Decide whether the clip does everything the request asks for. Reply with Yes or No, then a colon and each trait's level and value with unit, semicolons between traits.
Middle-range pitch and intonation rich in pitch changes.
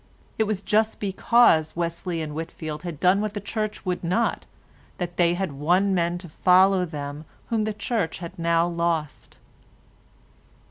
No: medium, 175 Hz; average, 3.3 semitones